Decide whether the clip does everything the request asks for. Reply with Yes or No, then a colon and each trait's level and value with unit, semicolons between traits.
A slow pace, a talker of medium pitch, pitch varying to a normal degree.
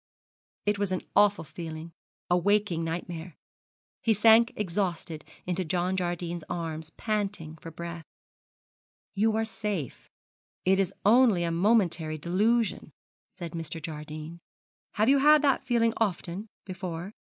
Yes: slow, 130 wpm; medium, 180 Hz; average, 4.1 semitones